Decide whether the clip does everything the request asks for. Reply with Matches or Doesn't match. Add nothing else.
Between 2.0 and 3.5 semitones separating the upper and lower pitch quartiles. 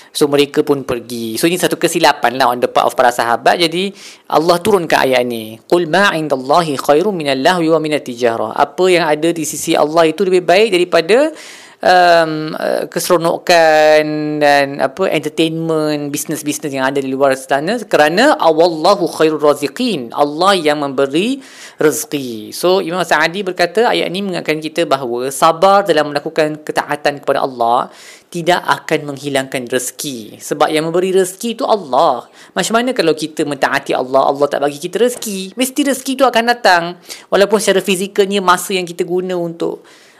Doesn't match